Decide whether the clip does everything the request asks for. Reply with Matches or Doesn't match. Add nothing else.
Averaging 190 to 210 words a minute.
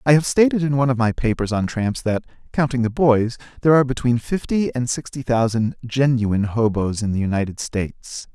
Matches